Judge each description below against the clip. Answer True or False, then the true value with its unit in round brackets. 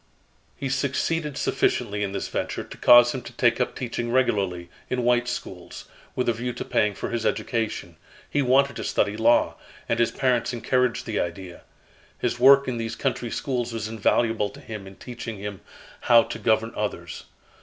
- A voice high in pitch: False (120 Hz)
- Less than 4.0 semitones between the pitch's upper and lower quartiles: True (3.0 semitones)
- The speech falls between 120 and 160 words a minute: False (180 wpm)